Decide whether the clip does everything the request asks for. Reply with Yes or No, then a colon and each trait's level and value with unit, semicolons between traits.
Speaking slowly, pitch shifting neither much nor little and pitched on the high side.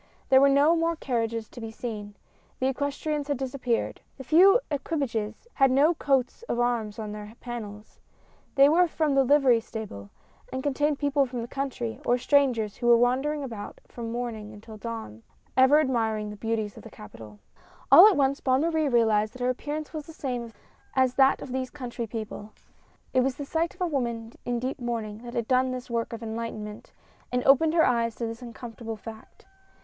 No: average, 200 wpm; average, 3.6 semitones; high, 245 Hz